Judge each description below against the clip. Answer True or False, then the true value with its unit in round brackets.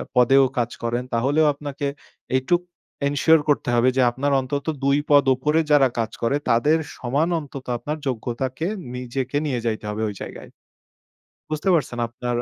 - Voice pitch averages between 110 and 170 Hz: True (135 Hz)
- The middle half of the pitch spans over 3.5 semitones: False (3.1 semitones)